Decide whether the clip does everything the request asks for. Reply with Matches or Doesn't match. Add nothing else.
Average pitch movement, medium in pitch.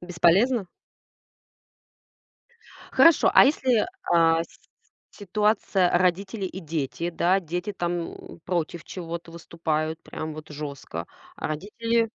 Matches